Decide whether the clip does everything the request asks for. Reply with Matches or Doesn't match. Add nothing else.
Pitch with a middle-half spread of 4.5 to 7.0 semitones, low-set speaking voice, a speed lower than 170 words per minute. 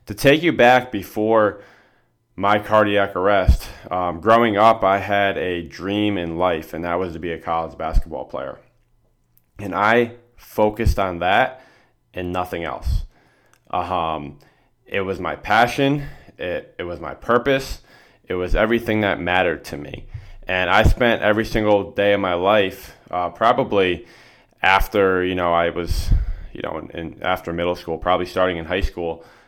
Doesn't match